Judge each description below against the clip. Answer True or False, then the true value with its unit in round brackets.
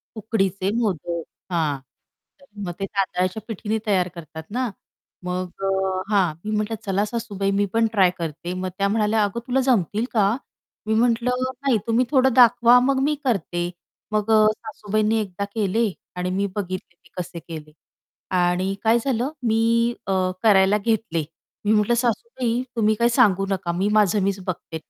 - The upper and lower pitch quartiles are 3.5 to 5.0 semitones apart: True (3.8 semitones)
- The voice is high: True (210 Hz)